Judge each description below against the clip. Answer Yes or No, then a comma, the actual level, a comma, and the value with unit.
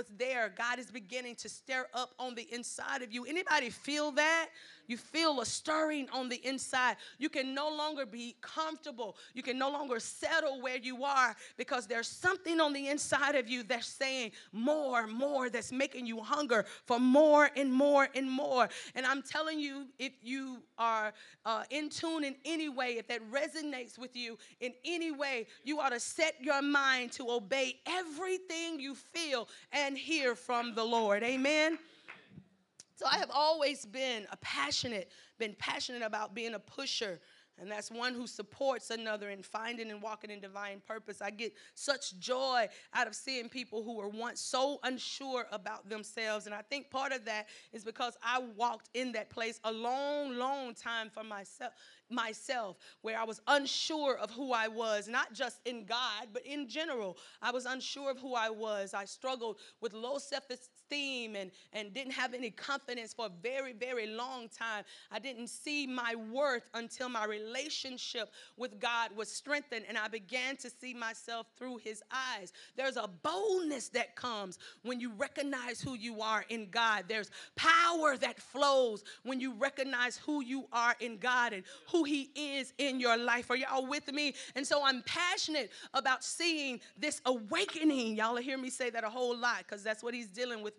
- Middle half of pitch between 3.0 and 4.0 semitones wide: Yes, average, 3.4 semitones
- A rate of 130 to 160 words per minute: No, average, 180 wpm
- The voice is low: No, very high, 250 Hz